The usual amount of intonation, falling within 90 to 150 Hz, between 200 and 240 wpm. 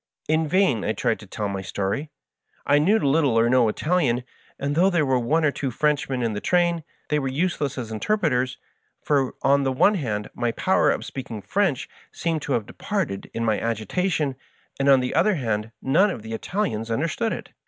No: wide, 6.0 semitones; low, 135 Hz; fast, 205 wpm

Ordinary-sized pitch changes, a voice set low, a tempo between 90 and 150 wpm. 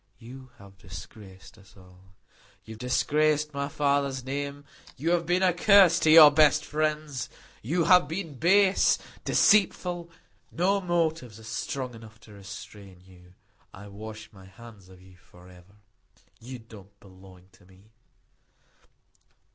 No: wide, 7.9 semitones; low, 125 Hz; average, 140 wpm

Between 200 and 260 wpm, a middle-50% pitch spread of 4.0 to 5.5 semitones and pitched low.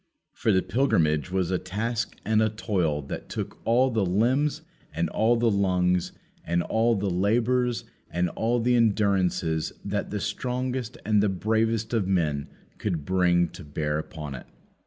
No: average, 160 wpm; average, 4.6 semitones; low, 100 Hz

